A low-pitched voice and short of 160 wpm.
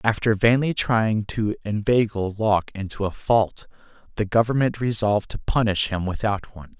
Yes: low, 105 Hz; average, 150 wpm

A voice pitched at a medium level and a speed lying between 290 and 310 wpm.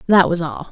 No: medium, 175 Hz; fast, 250 wpm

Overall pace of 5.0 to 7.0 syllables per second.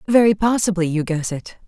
Yes: 5.6 syllables/s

